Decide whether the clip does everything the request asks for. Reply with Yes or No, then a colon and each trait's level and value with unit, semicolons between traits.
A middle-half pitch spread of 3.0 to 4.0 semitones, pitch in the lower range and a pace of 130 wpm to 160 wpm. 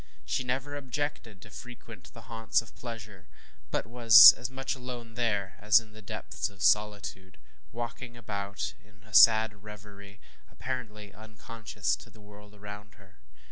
No: narrow, 2.4 semitones; low, 110 Hz; average, 150 wpm